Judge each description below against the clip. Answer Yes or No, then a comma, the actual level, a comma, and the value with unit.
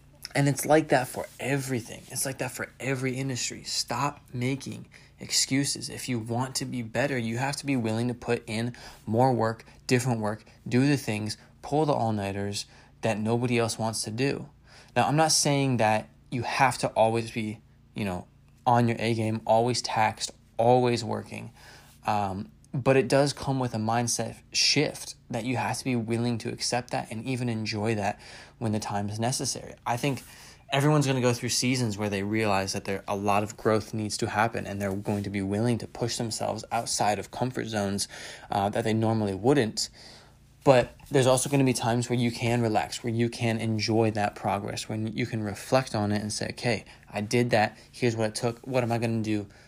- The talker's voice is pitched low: Yes, low, 120 Hz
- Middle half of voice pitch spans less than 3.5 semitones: Yes, average, 2.7 semitones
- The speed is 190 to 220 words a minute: Yes, average, 200 wpm